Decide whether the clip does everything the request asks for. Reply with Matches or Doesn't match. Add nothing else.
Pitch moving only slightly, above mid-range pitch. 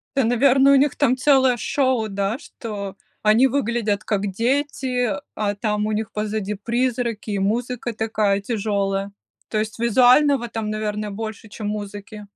Doesn't match